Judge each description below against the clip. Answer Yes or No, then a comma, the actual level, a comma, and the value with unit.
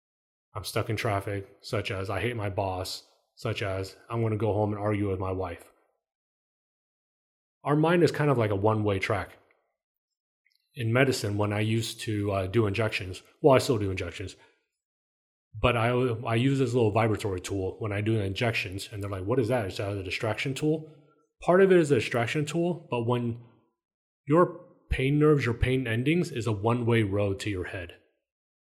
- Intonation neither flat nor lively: Yes, average, 4.3 semitones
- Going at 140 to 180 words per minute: No, average, 190 wpm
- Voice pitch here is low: Yes, low, 110 Hz